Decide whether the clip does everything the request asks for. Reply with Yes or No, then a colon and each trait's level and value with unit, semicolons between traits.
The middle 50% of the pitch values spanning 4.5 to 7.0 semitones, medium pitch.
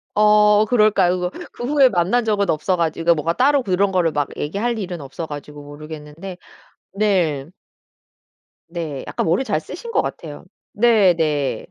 Yes: average, 5.3 semitones; medium, 180 Hz